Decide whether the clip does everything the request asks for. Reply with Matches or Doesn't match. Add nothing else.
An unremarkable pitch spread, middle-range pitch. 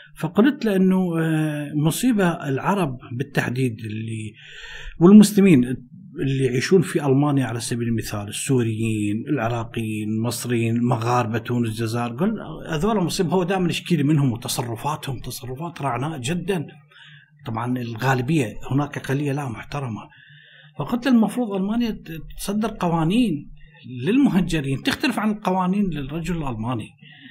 Doesn't match